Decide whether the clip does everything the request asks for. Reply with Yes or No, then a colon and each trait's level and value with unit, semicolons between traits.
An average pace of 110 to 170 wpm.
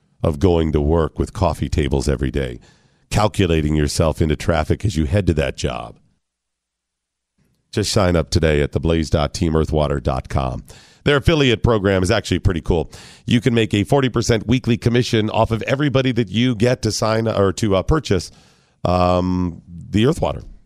Yes: average, 160 wpm